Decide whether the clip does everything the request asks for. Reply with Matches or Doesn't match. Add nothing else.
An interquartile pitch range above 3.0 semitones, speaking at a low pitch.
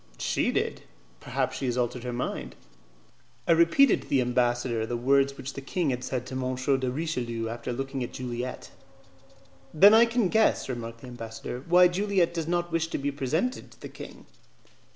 Matches